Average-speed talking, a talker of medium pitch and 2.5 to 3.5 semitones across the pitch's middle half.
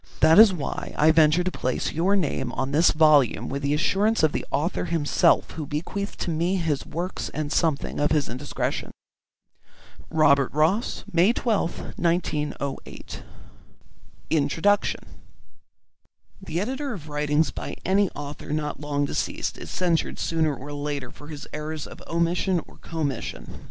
Yes: average, 145 wpm; medium, 155 Hz; average, 3.1 semitones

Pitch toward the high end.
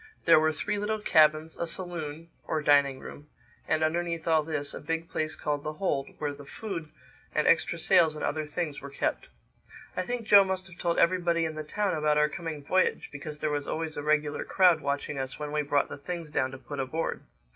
No: medium, 155 Hz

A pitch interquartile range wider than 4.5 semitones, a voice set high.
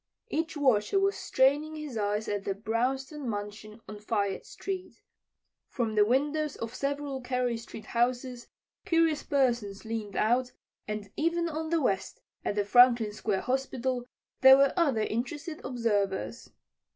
Yes: average, 5.1 semitones; very high, 250 Hz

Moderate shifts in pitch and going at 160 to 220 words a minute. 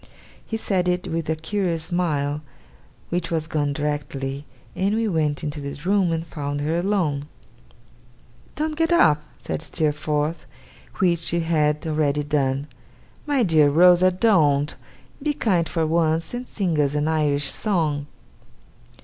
No: average, 3.5 semitones; average, 140 wpm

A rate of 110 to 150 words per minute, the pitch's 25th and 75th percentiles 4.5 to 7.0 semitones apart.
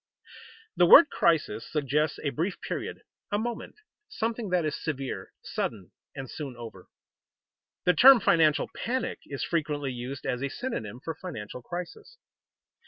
Yes: average, 145 wpm; wide, 5.6 semitones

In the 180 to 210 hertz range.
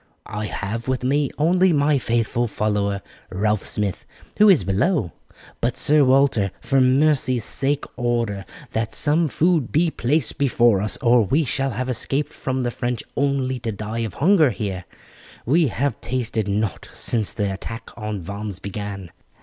No: low, 120 Hz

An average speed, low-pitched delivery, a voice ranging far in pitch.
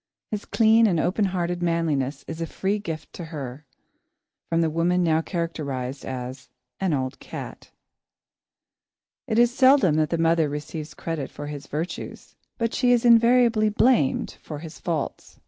No: average, 155 wpm; medium, 165 Hz; wide, 5.9 semitones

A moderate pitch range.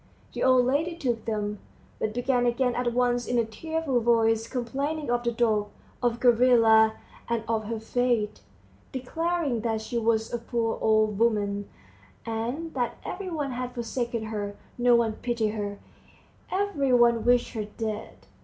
No: narrow, 2.1 semitones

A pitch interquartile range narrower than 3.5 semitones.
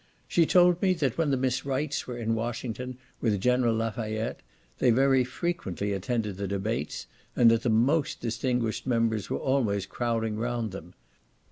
Yes: average, 3.0 semitones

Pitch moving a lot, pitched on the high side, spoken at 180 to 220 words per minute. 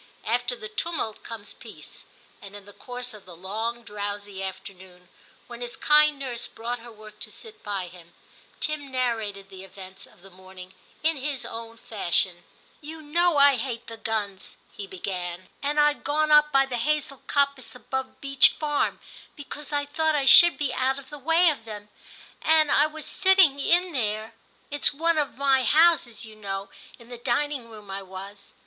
Yes: wide, 6.2 semitones; high, 240 Hz; average, 190 wpm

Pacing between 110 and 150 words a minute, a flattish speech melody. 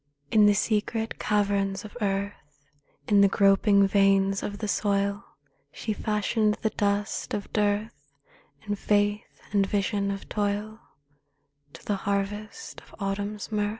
Yes: slow, 135 wpm; narrow, 1.0 semitones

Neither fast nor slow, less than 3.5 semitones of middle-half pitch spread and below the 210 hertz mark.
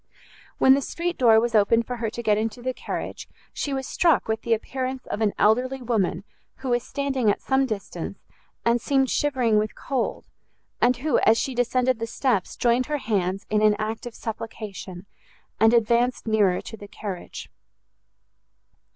No: average, 175 wpm; average, 3.1 semitones; high, 235 Hz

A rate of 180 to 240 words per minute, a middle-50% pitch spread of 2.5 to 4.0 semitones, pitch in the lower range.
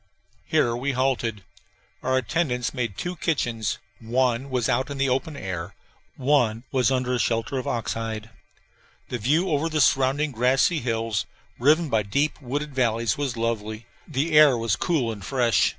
No: average, 165 wpm; average, 3.6 semitones; low, 125 Hz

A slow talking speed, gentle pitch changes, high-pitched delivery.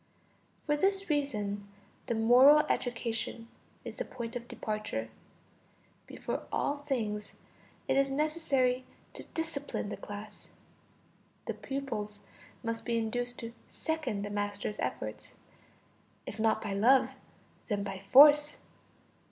No: slow, 120 wpm; average, 5.1 semitones; high, 235 Hz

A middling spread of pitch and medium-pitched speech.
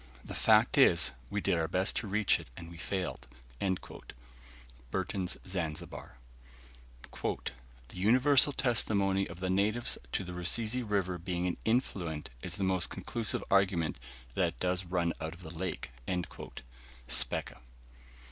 No: average, 3.0 semitones; very low, 95 Hz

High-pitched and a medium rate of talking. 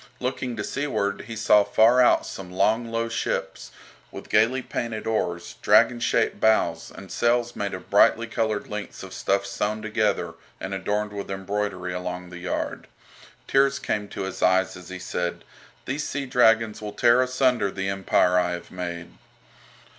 No: low, 105 Hz; average, 165 wpm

